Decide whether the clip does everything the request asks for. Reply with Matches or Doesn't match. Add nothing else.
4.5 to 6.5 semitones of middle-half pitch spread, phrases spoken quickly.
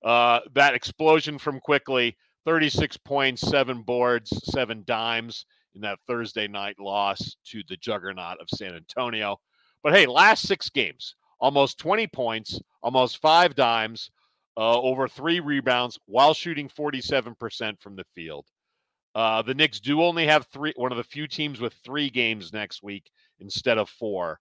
Doesn't match